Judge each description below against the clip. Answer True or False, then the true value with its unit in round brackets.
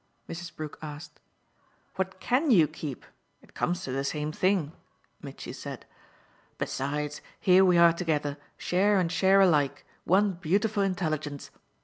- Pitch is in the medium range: True (170 Hz)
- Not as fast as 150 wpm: True (135 wpm)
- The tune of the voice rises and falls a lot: False (4.2 semitones)